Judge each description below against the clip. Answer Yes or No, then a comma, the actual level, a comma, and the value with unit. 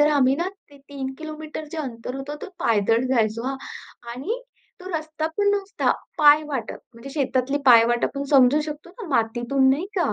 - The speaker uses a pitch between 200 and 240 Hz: No, very high, 280 Hz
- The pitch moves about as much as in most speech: Yes, average, 3.8 semitones